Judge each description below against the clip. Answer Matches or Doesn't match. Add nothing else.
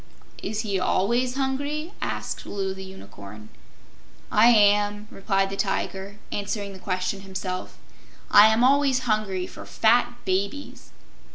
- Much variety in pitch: Doesn't match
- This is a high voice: Matches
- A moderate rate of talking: Doesn't match